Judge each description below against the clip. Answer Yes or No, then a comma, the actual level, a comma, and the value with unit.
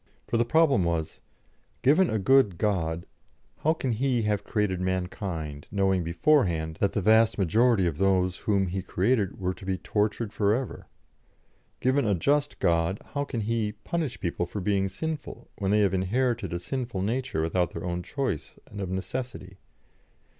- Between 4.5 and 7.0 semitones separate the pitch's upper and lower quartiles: Yes, average, 4.8 semitones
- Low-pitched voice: Yes, low, 100 Hz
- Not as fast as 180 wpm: Yes, average, 170 wpm